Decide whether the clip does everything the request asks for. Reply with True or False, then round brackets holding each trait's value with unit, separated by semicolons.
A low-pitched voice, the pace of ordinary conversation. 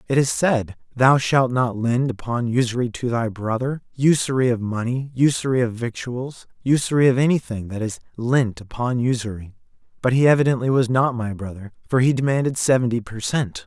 True (120 Hz; 170 wpm)